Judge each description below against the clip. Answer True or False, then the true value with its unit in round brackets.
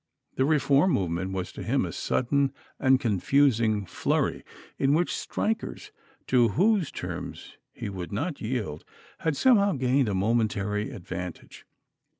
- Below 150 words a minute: True (135 wpm)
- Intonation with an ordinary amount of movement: False (6.2 semitones)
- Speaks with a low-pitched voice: True (125 Hz)